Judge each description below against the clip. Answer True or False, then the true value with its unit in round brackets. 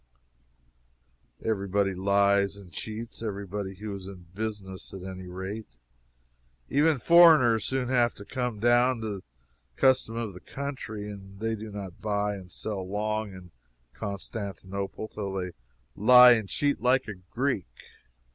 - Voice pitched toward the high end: False (105 Hz)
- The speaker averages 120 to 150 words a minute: True (145 wpm)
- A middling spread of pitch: True (3.2 semitones)